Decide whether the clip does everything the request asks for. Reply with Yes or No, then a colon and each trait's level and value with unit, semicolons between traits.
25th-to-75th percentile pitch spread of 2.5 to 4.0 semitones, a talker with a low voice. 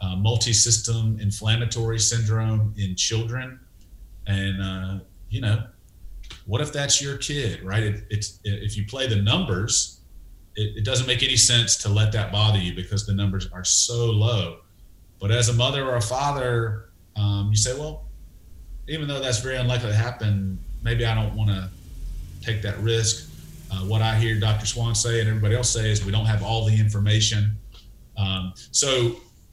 Yes: average, 3.0 semitones; low, 105 Hz